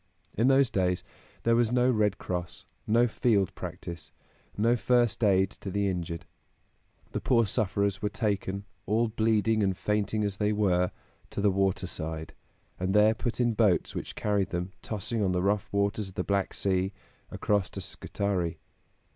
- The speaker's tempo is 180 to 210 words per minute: No, average, 165 wpm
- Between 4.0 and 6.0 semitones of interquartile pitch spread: No, average, 2.7 semitones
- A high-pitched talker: No, low, 100 Hz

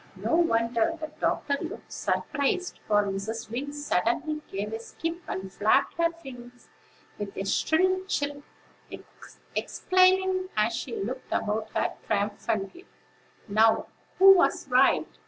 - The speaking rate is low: Yes, slow, 125 wpm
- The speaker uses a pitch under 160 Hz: No, very high, 250 Hz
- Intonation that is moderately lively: No, wide, 7.4 semitones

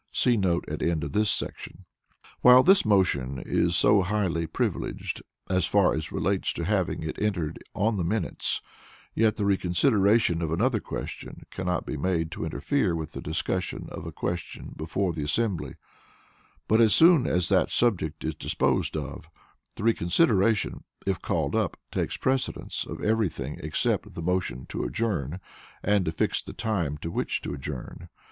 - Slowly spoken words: No, average, 165 wpm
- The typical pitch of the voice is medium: No, very low, 90 Hz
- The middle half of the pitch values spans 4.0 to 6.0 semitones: Yes, average, 4.7 semitones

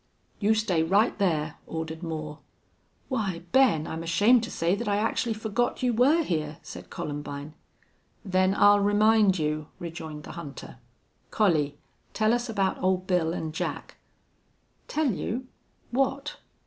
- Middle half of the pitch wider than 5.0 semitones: Yes, wide, 5.6 semitones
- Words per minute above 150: No, average, 140 wpm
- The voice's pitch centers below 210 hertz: Yes, high, 190 Hz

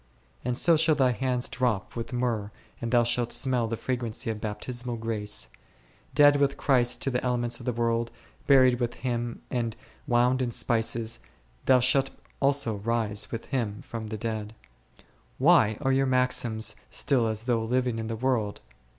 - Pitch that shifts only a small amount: Yes, narrow, 2.2 semitones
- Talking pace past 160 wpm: Yes, average, 170 wpm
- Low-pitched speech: Yes, low, 120 Hz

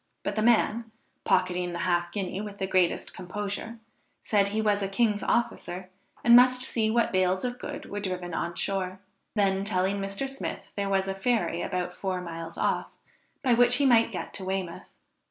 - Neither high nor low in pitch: No, high, 195 Hz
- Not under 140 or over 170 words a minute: No, average, 185 wpm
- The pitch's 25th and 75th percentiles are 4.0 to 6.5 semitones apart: No, average, 3.5 semitones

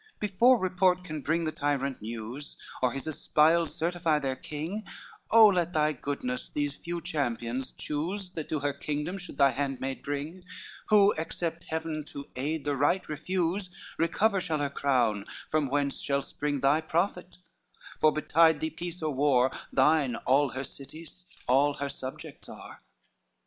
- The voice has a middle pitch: Yes, medium, 150 Hz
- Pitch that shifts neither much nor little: Yes, average, 3.7 semitones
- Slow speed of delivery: No, average, 160 wpm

